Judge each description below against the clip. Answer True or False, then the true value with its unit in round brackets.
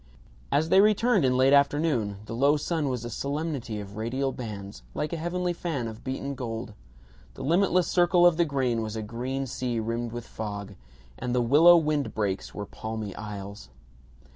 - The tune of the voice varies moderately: False (5.9 semitones)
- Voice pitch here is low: True (130 Hz)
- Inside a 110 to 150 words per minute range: False (180 wpm)